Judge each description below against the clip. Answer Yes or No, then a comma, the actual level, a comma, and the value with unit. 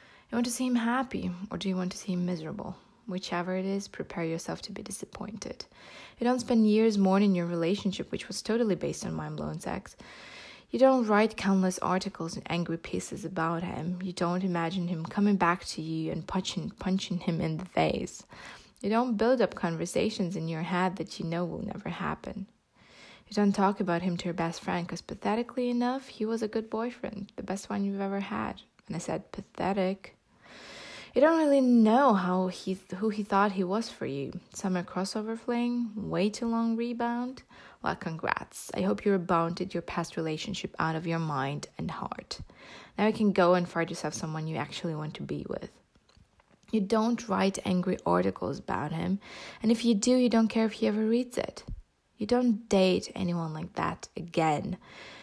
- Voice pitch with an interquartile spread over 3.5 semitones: Yes, average, 4.2 semitones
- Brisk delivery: No, average, 195 wpm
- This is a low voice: No, high, 190 Hz